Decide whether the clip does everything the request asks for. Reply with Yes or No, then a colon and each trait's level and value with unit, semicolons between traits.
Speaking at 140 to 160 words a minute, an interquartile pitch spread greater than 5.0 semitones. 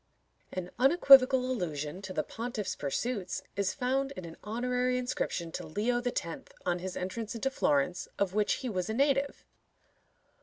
Yes: average, 155 wpm; wide, 5.6 semitones